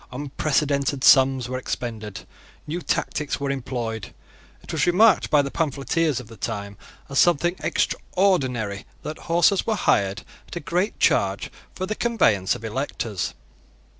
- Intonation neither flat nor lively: No, wide, 6.4 semitones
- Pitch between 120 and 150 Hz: Yes, medium, 140 Hz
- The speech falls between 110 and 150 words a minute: Yes, average, 140 wpm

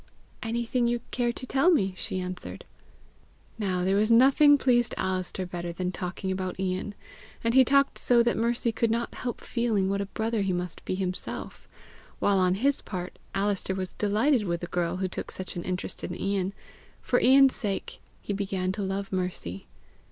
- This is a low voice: No, high, 200 Hz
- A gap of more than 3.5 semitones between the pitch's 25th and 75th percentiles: Yes, average, 4.2 semitones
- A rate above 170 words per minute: Yes, average, 180 wpm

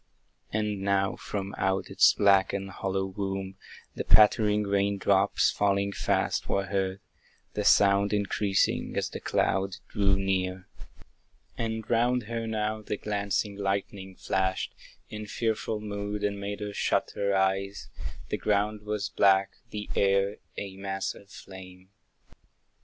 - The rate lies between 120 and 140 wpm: Yes, slow, 135 wpm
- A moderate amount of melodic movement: No, narrow, 1.3 semitones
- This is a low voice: Yes, low, 100 Hz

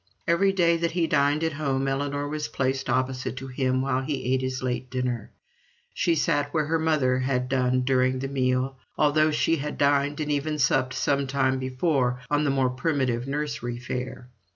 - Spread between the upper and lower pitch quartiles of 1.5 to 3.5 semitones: Yes, narrow, 2.5 semitones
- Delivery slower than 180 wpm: No, average, 185 wpm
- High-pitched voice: No, low, 135 Hz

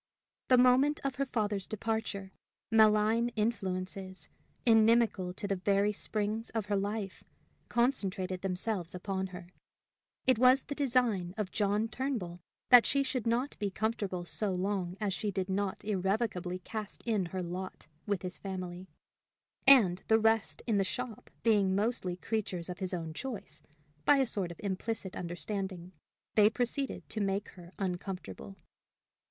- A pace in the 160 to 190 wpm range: No, average, 145 wpm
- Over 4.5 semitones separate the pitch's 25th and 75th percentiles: No, average, 3.4 semitones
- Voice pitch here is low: No, high, 205 Hz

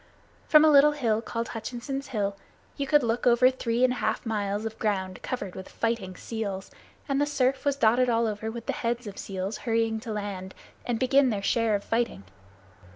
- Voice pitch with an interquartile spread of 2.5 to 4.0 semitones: Yes, average, 3.5 semitones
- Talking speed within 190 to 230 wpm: Yes, fast, 205 wpm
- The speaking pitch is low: No, high, 230 Hz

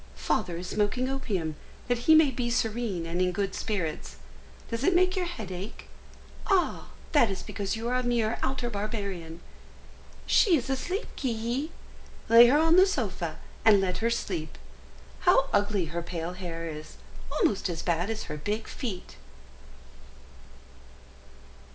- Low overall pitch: No, high, 220 Hz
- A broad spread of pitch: Yes, wide, 5.9 semitones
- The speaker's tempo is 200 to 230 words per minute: No, average, 155 wpm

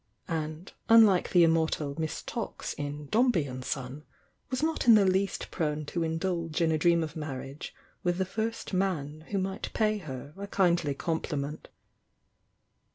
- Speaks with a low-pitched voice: No, medium, 165 Hz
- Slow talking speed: No, average, 160 wpm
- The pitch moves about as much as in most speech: Yes, average, 4.3 semitones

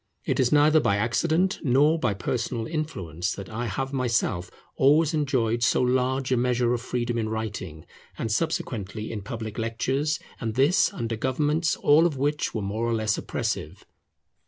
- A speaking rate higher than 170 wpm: No, average, 165 wpm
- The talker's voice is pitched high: No, low, 120 Hz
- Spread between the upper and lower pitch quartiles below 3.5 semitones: No, average, 4.8 semitones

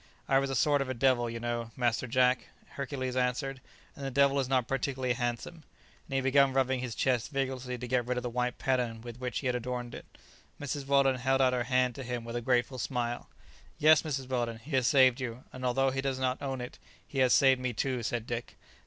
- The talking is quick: Yes, fast, 230 wpm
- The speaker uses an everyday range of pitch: No, narrow, 1.7 semitones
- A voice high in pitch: No, low, 130 Hz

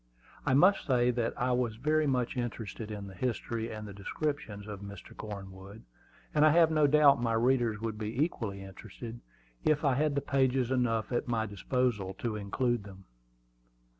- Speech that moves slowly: No, average, 165 wpm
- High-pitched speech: No, low, 120 Hz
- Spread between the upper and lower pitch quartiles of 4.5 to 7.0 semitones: No, average, 3.9 semitones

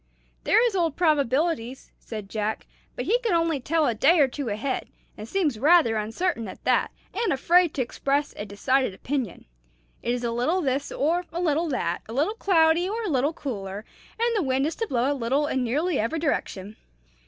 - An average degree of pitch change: No, wide, 6.3 semitones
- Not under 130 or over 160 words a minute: No, average, 200 wpm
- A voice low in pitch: No, very high, 280 Hz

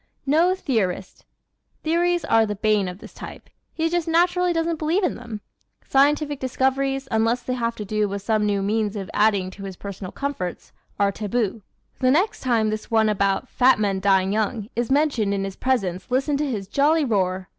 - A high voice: Yes, high, 225 Hz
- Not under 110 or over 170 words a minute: No, average, 190 wpm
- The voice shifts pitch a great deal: Yes, wide, 5.9 semitones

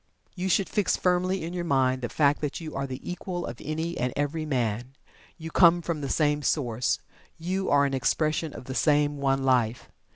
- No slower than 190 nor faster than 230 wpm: Yes, average, 200 wpm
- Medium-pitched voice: Yes, medium, 145 Hz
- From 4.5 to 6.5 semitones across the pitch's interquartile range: No, average, 4.1 semitones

